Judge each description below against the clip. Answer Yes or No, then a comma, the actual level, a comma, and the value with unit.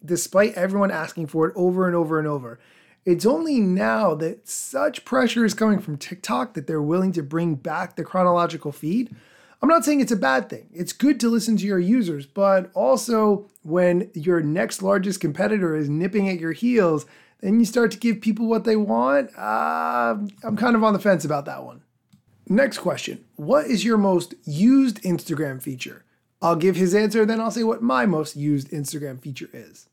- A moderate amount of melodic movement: No, wide, 5.9 semitones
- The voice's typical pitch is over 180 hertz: Yes, high, 190 Hz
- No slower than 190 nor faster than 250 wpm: Yes, average, 195 wpm